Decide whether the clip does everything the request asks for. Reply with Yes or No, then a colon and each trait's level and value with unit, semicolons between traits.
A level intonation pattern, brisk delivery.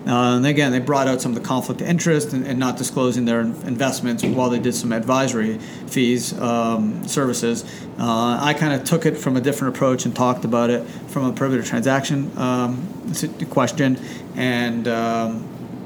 No: narrow, 2.2 semitones; average, 180 wpm